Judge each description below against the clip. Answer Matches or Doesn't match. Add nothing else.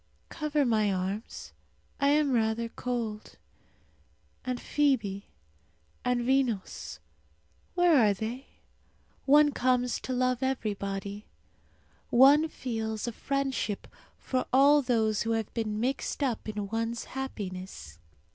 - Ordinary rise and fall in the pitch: Matches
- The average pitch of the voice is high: Matches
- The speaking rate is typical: Doesn't match